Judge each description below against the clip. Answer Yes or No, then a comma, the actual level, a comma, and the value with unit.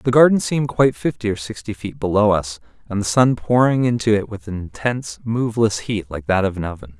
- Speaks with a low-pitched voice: Yes, low, 110 Hz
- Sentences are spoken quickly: Yes, fast, 225 wpm